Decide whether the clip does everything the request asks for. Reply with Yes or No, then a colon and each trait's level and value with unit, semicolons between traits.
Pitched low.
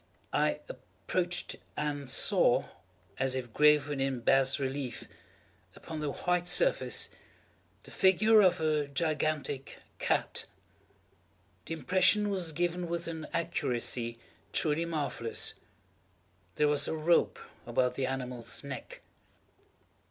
No: medium, 150 Hz